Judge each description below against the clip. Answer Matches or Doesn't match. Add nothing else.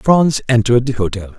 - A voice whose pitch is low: Matches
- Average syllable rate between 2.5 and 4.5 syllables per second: Doesn't match